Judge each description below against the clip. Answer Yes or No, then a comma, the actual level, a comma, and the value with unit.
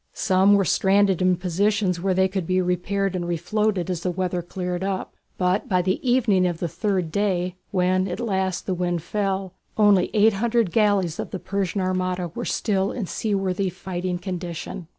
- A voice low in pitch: No, medium, 185 Hz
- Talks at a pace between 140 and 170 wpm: No, average, 180 wpm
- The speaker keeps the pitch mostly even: Yes, narrow, 1.8 semitones